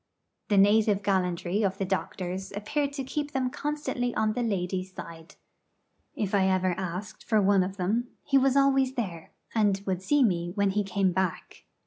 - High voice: Yes, high, 200 Hz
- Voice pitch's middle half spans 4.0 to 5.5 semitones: Yes, average, 4.5 semitones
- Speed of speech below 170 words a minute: No, average, 175 wpm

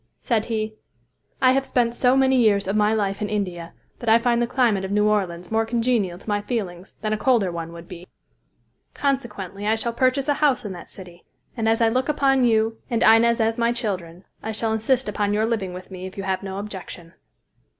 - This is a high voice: Yes, high, 220 Hz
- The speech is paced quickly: Yes, fast, 220 wpm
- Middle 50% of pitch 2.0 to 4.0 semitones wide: Yes, average, 3.6 semitones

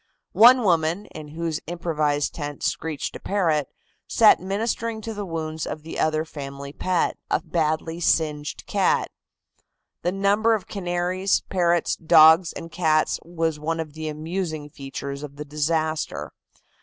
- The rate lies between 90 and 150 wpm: Yes, average, 145 wpm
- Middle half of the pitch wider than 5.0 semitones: No, average, 2.8 semitones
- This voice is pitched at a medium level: Yes, medium, 160 Hz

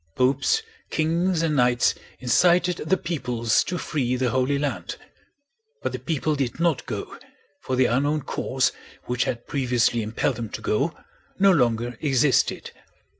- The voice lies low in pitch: Yes, low, 130 Hz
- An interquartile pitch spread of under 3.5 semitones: No, average, 4.5 semitones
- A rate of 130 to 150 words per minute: Yes, average, 145 wpm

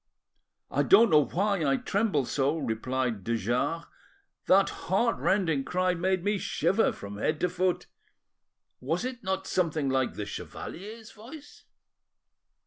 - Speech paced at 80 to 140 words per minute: Yes, slow, 135 wpm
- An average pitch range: No, wide, 6.7 semitones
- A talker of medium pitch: Yes, medium, 175 Hz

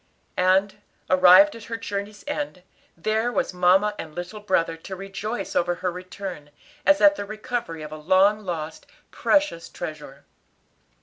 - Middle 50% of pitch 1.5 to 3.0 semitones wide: No, average, 3.6 semitones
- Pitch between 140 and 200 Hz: Yes, high, 190 Hz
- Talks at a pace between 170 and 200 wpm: No, average, 145 wpm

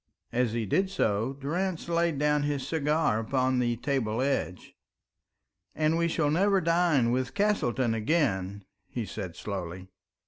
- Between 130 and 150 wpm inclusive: Yes, average, 140 wpm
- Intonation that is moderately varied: No, wide, 6.3 semitones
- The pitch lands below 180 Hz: Yes, low, 135 Hz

